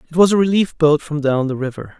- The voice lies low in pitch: No, medium, 155 Hz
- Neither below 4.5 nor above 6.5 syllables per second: Yes, 6.2 syllables/s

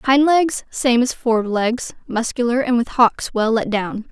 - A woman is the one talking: Yes, female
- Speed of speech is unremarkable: Yes, average, 175 wpm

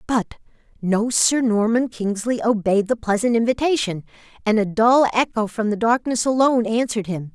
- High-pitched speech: Yes, high, 225 Hz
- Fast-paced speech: No, average, 155 wpm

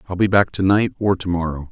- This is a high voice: No, very low, 95 Hz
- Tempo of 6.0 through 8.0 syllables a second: Yes, 6.2 syllables/s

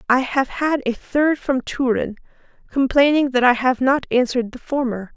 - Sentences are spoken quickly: No, average, 175 wpm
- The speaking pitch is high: Yes, very high, 260 Hz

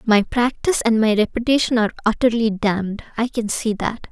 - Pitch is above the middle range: Yes, high, 225 Hz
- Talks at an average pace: Yes, average, 160 wpm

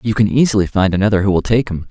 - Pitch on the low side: Yes, low, 100 Hz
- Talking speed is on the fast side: Yes, fast, 285 wpm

